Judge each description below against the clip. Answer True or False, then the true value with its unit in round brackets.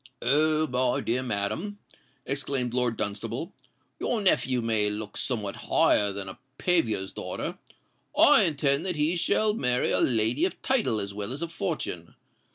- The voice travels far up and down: True (6.4 semitones)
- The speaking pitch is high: False (125 Hz)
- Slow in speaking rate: False (155 wpm)